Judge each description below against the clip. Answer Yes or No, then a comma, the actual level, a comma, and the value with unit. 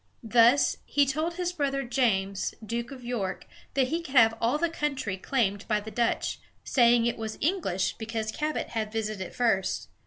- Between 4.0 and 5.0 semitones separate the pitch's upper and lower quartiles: Yes, average, 4.3 semitones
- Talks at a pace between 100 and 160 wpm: No, average, 185 wpm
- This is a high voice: Yes, high, 235 Hz